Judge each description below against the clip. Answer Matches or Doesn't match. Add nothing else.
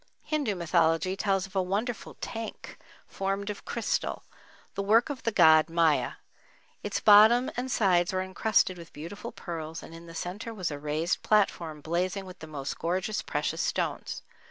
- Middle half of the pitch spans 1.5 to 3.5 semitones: Doesn't match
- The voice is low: Doesn't match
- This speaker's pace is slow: Doesn't match